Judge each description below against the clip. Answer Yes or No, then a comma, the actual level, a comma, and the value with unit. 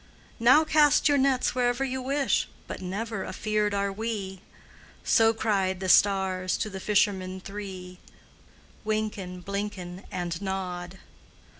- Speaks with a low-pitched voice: No, high, 200 Hz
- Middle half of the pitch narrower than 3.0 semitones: No, average, 3.3 semitones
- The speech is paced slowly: Yes, slow, 125 wpm